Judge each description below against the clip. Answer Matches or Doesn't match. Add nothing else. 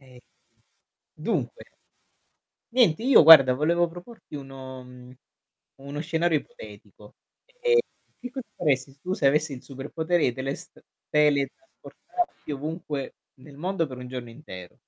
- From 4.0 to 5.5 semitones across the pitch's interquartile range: Matches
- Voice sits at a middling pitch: Matches